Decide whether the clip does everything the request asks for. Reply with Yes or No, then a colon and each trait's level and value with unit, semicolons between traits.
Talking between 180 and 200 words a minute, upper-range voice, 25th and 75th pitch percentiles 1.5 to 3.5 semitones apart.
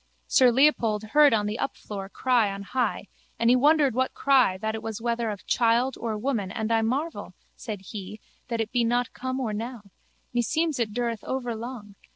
Yes: average, 190 wpm; high, 230 Hz; average, 3.2 semitones